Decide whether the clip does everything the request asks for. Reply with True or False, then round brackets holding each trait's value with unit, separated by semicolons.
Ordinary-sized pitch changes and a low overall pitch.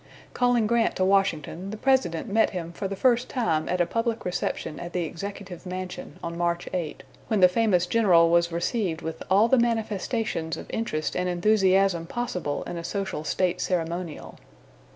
False (4.2 semitones; 185 Hz)